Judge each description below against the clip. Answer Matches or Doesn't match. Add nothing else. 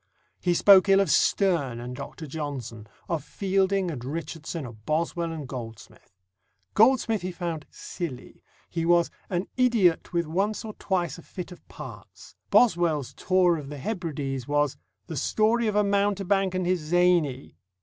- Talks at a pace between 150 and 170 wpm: Matches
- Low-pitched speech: Doesn't match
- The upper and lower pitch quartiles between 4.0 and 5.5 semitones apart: Matches